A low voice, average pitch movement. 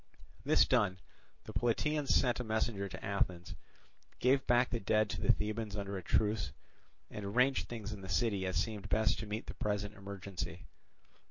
Yes: low, 105 Hz; average, 3.0 semitones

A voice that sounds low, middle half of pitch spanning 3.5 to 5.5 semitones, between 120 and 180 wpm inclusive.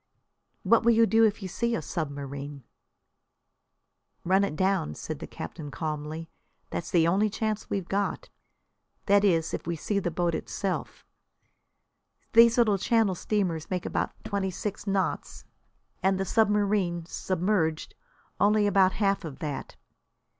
No: high, 190 Hz; average, 4.1 semitones; average, 140 wpm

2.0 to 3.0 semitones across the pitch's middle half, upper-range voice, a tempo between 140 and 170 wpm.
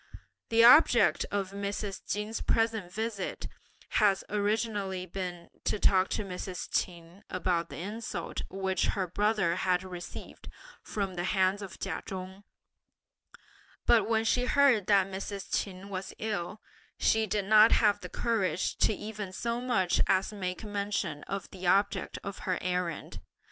Yes: narrow, 2.5 semitones; high, 195 Hz; average, 145 wpm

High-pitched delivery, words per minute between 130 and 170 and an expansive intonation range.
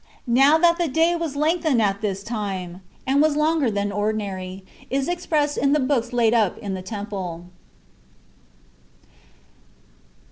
Yes: high, 240 Hz; average, 140 wpm; wide, 7.0 semitones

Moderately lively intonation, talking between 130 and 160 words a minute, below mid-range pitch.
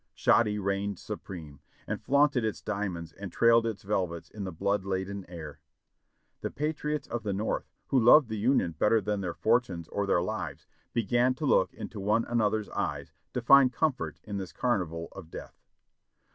No: average, 4.0 semitones; average, 175 wpm; low, 105 Hz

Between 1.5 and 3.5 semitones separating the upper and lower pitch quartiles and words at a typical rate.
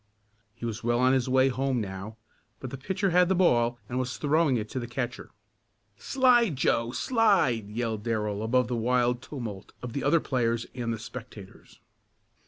Yes: average, 2.8 semitones; average, 180 wpm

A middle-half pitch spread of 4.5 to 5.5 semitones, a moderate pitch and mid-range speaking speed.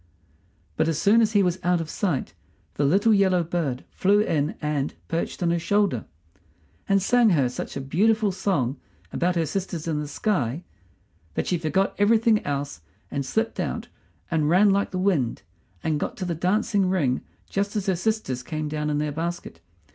Yes: average, 5.0 semitones; medium, 175 Hz; average, 185 wpm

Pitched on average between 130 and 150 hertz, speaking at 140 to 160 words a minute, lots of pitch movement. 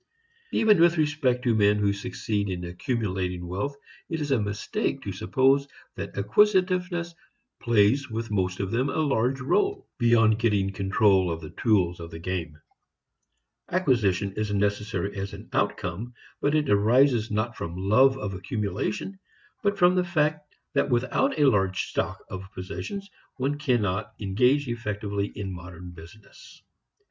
No: low, 110 Hz; average, 150 wpm; wide, 6.2 semitones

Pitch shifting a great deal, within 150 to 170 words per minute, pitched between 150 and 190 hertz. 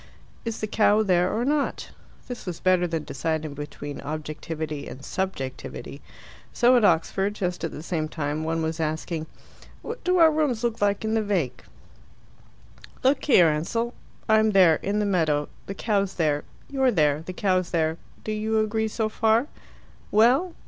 Yes: wide, 5.7 semitones; average, 165 wpm; medium, 185 Hz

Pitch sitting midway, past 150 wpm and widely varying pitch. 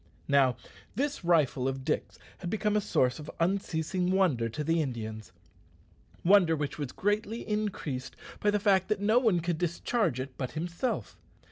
Yes: medium, 170 Hz; average, 160 wpm; wide, 7.0 semitones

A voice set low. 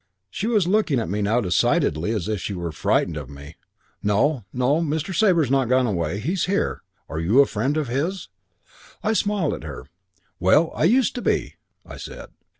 Yes: low, 130 Hz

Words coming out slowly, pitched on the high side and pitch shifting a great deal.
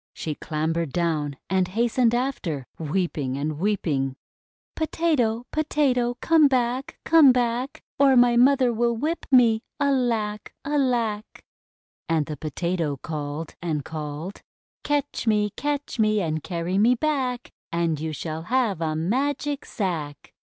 Yes: slow, 130 wpm; high, 215 Hz; wide, 8.0 semitones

